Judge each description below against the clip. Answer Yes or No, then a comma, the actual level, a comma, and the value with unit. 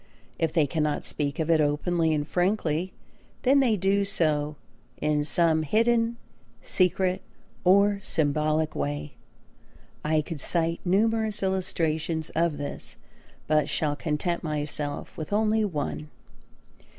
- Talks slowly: Yes, slow, 120 wpm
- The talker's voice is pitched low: No, medium, 160 Hz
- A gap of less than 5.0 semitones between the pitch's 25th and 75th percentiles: Yes, average, 4.2 semitones